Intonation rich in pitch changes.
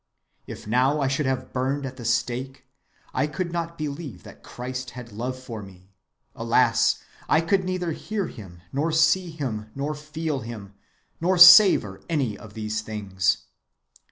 Yes: wide, 6.1 semitones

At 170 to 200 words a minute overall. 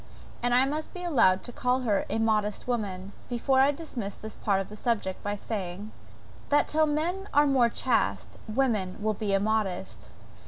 Yes: average, 180 wpm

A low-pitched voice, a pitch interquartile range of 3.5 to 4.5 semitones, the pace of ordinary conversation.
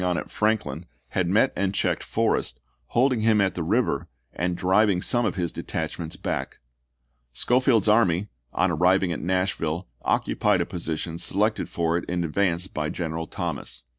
Yes: very low, 90 Hz; average, 3.9 semitones; average, 160 wpm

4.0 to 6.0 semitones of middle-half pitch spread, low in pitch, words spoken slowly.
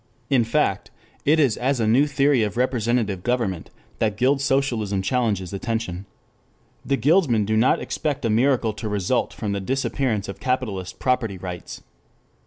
No: average, 4.4 semitones; low, 115 Hz; average, 155 wpm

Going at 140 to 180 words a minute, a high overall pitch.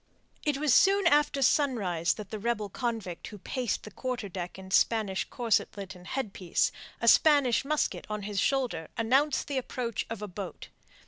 Yes: average, 170 wpm; high, 225 Hz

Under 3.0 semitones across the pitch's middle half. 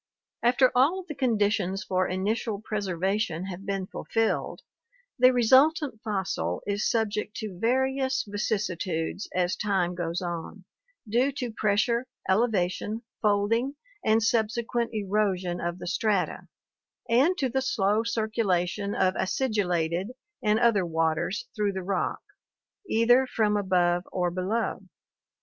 No: average, 4.0 semitones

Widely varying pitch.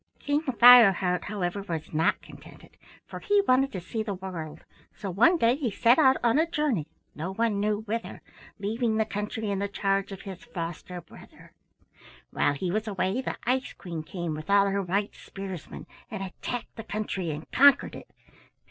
No: average, 4.3 semitones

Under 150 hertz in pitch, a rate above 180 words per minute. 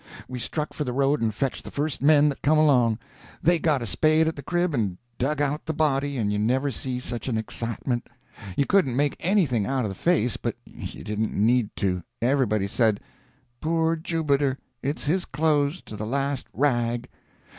Yes: low, 135 Hz; average, 190 wpm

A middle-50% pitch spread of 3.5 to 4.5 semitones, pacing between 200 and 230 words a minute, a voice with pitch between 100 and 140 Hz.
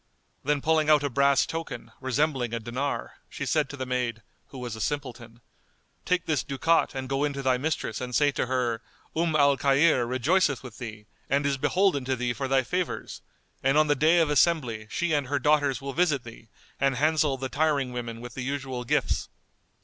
No: average, 3.1 semitones; fast, 205 wpm; low, 135 Hz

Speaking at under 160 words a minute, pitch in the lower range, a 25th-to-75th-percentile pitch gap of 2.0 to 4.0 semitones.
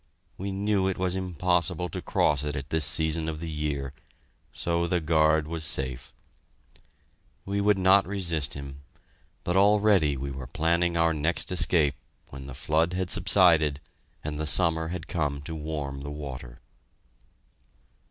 Yes: average, 150 wpm; very low, 80 Hz; average, 3.5 semitones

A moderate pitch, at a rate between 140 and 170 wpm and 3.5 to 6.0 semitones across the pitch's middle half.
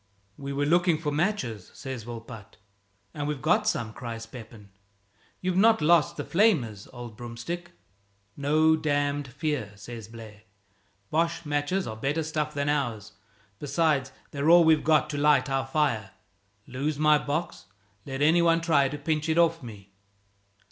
Yes: medium, 145 Hz; average, 155 wpm; average, 4.9 semitones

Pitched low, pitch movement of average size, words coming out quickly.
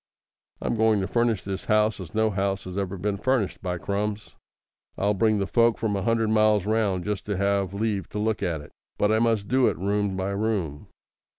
No: low, 105 Hz; narrow, 2.2 semitones; fast, 210 wpm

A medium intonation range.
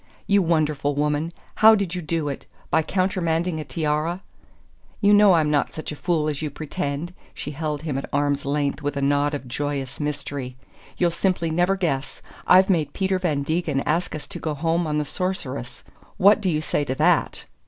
Yes: average, 3.4 semitones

